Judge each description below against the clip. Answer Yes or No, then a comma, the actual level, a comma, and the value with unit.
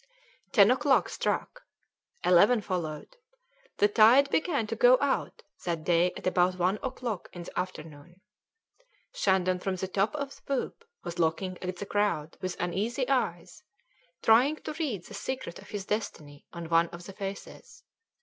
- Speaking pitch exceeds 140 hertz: Yes, high, 190 Hz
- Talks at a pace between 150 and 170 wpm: Yes, average, 160 wpm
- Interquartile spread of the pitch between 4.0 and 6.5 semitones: Yes, average, 5.1 semitones